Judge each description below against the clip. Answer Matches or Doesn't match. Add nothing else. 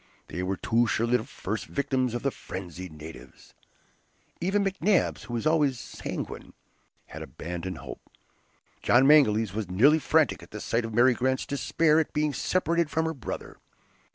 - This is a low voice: Matches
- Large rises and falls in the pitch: Matches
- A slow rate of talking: Doesn't match